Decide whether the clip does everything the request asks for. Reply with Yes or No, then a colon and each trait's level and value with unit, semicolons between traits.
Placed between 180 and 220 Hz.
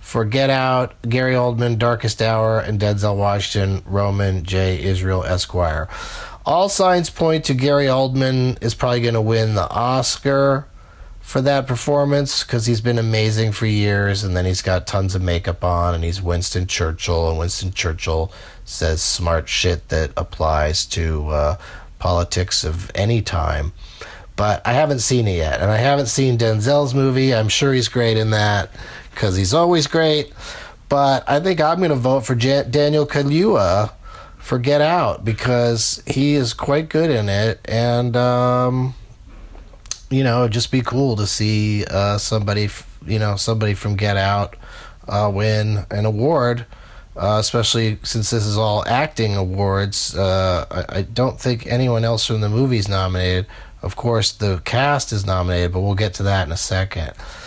No: low, 110 Hz